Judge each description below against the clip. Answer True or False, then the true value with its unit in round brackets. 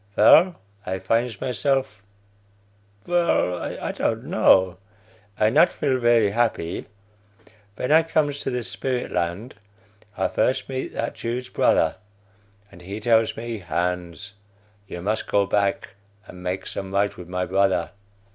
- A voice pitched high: False (110 Hz)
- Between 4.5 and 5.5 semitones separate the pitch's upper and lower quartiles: True (5.2 semitones)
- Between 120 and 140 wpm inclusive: True (135 wpm)